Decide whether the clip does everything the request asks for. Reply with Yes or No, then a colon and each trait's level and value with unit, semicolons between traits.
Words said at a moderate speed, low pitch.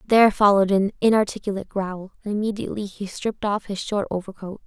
No: average, 165 wpm; high, 200 Hz